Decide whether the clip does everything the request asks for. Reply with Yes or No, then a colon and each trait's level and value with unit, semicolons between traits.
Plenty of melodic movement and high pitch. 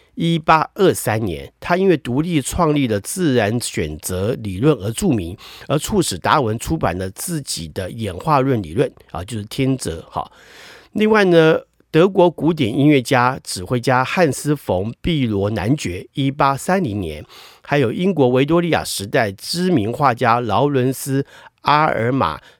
No: wide, 7.0 semitones; low, 130 Hz